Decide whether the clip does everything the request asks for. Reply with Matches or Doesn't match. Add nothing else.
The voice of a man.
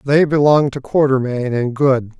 Matches